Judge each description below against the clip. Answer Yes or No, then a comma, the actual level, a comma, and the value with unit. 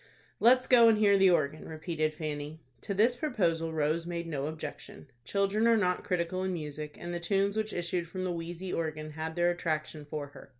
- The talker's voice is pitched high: No, medium, 170 Hz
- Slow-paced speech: No, average, 200 wpm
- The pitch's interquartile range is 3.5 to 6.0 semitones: Yes, average, 3.9 semitones